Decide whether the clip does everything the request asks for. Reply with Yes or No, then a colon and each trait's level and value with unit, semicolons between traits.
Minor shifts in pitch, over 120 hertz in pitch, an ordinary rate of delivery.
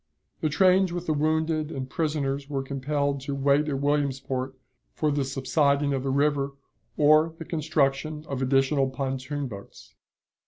Yes: narrow, 2.1 semitones; medium, 140 Hz; average, 150 wpm